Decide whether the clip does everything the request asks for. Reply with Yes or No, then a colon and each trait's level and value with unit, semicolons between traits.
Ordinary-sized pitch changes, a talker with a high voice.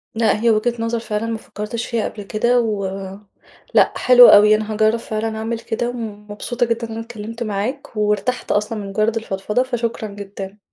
No: narrow, 1.8 semitones; high, 220 Hz